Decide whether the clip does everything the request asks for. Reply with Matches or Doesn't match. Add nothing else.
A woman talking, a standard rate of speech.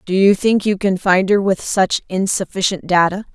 Matches